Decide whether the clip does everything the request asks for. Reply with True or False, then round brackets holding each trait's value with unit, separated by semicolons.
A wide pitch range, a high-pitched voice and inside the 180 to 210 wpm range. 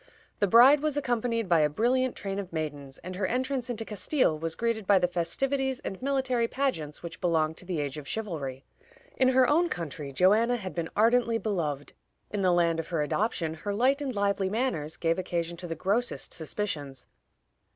True (6.8 semitones; 195 Hz; 190 wpm)